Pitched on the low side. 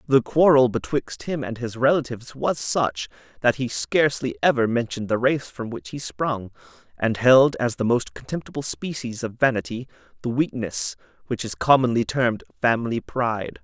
Yes: low, 120 Hz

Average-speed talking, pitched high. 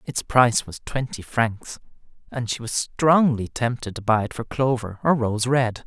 No: average, 185 wpm; low, 120 Hz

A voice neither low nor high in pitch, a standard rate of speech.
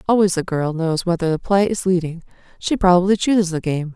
No: medium, 180 Hz; fast, 215 wpm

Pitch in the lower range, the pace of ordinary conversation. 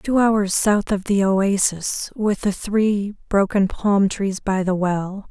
No: high, 200 Hz; average, 170 wpm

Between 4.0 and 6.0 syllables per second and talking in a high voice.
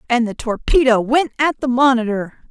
Yes: 5.0 syllables/s; high, 245 Hz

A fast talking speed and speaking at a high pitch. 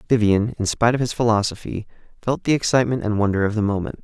No: fast, 210 wpm; low, 110 Hz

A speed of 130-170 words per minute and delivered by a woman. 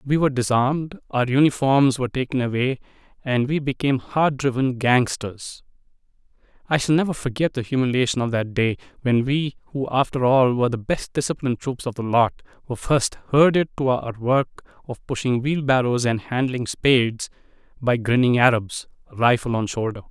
No: average, 160 wpm; male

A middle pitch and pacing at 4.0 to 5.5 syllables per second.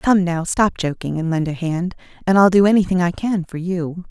Yes: medium, 180 Hz; 5.1 syllables/s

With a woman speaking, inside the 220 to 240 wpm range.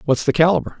No: male; fast, 225 wpm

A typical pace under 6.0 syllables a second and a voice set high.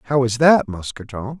No: 5.0 syllables/s; low, 125 Hz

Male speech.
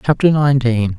Yes: male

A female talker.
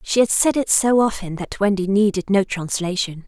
Yes: female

